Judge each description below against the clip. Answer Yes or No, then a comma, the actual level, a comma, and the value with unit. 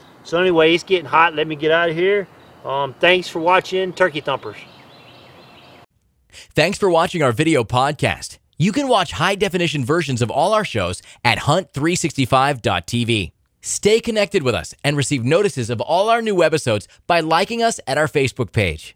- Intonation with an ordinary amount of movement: No, wide, 6.7 semitones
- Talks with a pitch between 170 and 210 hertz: No, medium, 155 Hz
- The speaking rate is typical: Yes, average, 170 wpm